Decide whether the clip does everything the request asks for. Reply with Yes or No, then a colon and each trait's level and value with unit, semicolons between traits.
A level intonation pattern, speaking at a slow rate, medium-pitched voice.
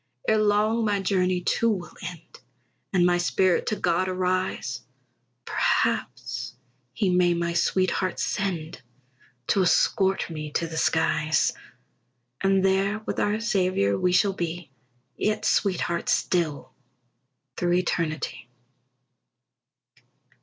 Yes: narrow, 2.3 semitones; slow, 110 wpm; medium, 180 Hz